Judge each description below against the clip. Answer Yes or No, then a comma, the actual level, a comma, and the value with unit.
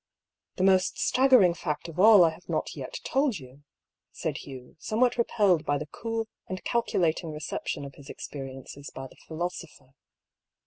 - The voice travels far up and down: Yes, wide, 6.7 semitones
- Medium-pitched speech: Yes, medium, 170 Hz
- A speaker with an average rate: Yes, average, 160 wpm